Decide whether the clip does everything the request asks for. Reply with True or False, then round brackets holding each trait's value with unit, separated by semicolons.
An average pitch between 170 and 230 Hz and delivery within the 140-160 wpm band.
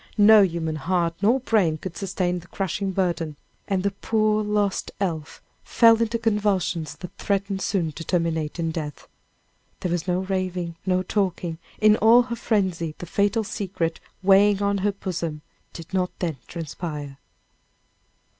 True (185 Hz; 150 wpm)